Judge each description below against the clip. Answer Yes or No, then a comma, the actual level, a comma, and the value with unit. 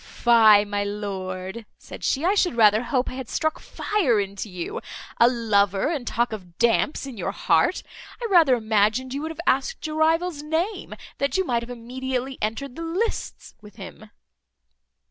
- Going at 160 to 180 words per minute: Yes, average, 175 wpm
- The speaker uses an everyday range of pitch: No, wide, 6.4 semitones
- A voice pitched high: Yes, high, 240 Hz